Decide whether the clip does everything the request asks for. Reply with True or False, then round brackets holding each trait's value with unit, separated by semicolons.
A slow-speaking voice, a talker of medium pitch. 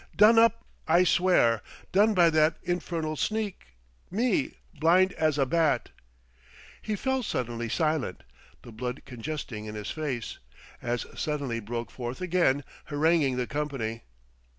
True (130 wpm; 155 Hz)